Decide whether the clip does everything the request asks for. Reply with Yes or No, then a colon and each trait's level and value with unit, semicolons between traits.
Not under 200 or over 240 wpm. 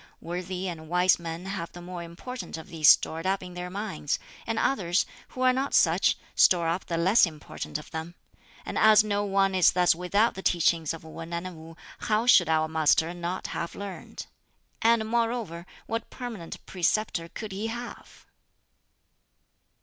No: average, 170 wpm